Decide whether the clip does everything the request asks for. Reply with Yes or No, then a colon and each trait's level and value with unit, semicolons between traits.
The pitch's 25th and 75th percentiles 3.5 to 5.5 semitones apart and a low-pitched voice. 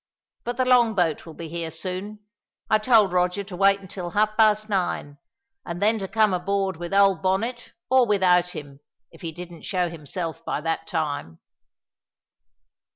No: average, 3.8 semitones; medium, 185 Hz